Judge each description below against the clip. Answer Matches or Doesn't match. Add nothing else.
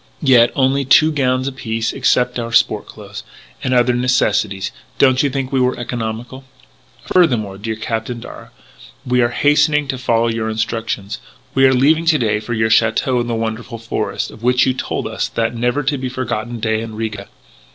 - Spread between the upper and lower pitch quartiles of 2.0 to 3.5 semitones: Matches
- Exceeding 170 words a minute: Matches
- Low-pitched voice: Matches